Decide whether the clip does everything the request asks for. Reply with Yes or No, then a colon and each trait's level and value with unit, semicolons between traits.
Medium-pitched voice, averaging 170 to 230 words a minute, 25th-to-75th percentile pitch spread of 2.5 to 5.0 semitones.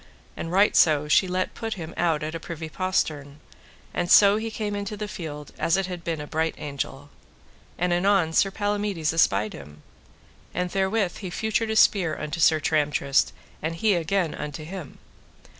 Yes: medium, 170 Hz; average, 175 wpm; average, 4.3 semitones